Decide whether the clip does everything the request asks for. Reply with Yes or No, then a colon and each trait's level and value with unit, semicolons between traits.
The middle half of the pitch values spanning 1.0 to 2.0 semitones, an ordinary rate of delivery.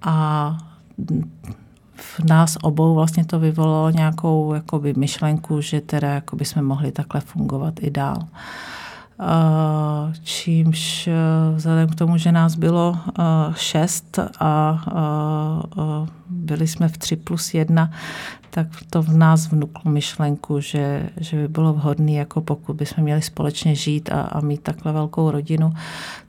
Yes: narrow, 1.5 semitones; average, 130 wpm